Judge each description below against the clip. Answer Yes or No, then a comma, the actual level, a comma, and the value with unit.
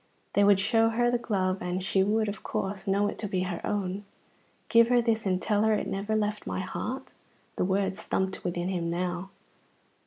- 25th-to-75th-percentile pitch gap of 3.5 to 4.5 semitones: No, average, 2.7 semitones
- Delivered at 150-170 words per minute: No, fast, 205 wpm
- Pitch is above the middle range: Yes, high, 200 Hz